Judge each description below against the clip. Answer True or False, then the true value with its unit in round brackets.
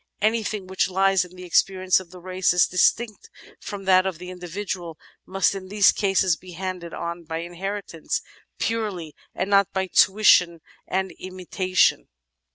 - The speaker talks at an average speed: True (160 wpm)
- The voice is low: False (185 Hz)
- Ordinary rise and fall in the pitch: False (1.5 semitones)